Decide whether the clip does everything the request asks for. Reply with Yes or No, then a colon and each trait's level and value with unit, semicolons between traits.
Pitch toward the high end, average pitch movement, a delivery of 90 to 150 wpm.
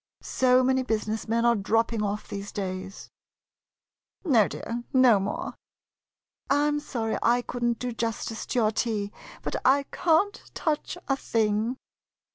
Yes: high, 230 Hz; average, 3.3 semitones; average, 145 wpm